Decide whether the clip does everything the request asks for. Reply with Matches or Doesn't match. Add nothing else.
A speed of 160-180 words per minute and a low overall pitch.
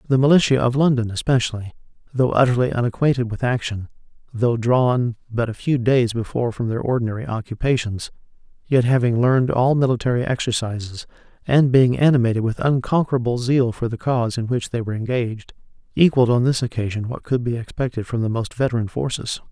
Matches